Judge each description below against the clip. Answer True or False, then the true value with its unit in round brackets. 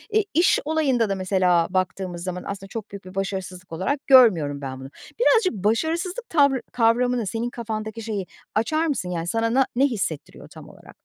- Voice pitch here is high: True (220 Hz)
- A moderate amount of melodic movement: False (6.0 semitones)